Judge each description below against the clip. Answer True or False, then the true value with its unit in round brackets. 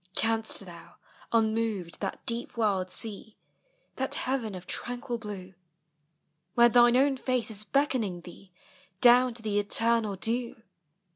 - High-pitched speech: True (225 Hz)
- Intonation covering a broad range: False (3.2 semitones)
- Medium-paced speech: False (130 wpm)